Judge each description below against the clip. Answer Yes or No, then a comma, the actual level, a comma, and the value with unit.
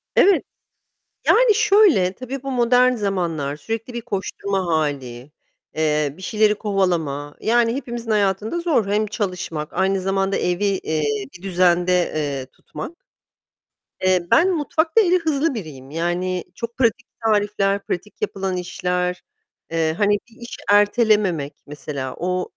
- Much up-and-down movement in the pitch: Yes, wide, 5.7 semitones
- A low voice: No, high, 195 Hz